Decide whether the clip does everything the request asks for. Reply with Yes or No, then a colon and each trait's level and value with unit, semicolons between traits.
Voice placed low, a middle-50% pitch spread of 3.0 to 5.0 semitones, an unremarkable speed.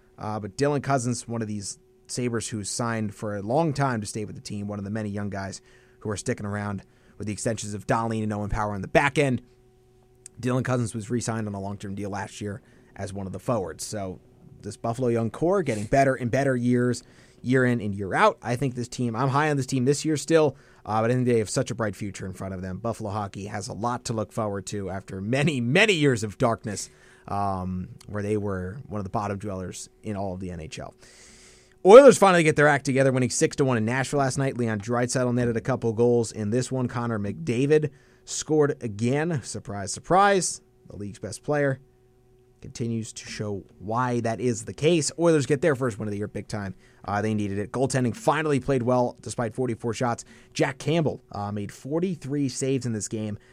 No: low, 120 Hz; average, 4.0 semitones; fast, 220 wpm